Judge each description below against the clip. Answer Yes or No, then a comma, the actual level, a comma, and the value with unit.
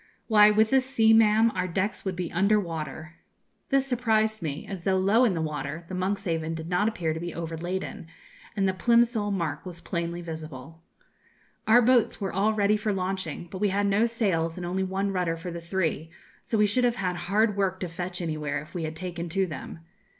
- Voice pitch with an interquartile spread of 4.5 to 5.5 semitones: No, average, 4.1 semitones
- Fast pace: Yes, fast, 210 wpm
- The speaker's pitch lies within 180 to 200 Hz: Yes, medium, 185 Hz